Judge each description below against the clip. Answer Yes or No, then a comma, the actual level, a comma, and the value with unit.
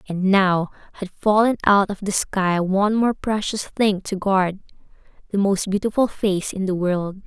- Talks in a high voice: Yes, high, 195 Hz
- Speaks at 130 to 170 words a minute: Yes, average, 165 wpm